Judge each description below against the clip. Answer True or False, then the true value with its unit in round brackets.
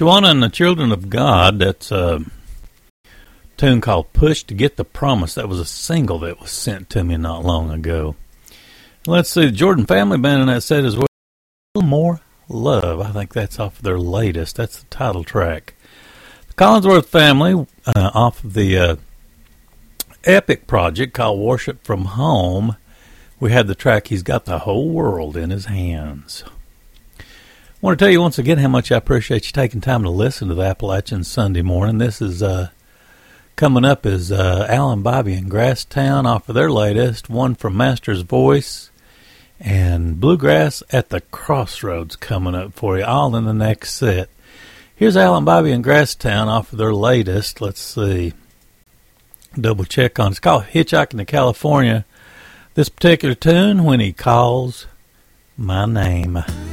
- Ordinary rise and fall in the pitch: False (6.0 semitones)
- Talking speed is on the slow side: False (170 wpm)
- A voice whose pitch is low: True (110 Hz)